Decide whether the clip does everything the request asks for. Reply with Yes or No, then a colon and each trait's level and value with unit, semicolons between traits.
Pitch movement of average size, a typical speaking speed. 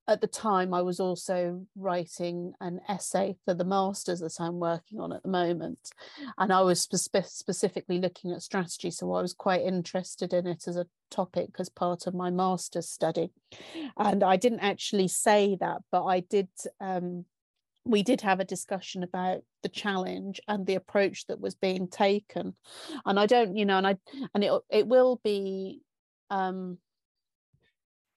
No: narrow, 2.1 semitones; average, 175 wpm